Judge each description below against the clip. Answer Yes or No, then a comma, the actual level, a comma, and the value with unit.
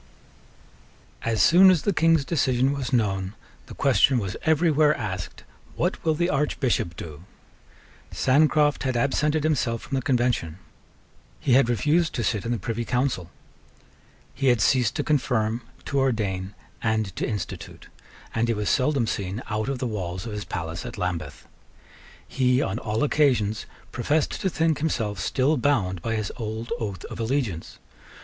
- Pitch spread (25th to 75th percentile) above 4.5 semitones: Yes, average, 5.2 semitones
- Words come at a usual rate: Yes, average, 160 wpm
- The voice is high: No, low, 120 Hz